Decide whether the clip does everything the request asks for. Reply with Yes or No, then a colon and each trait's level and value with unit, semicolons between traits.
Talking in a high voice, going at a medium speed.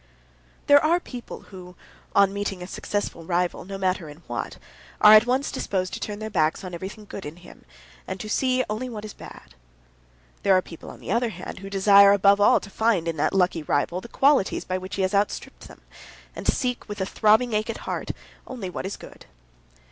No: high, 200 Hz; fast, 210 wpm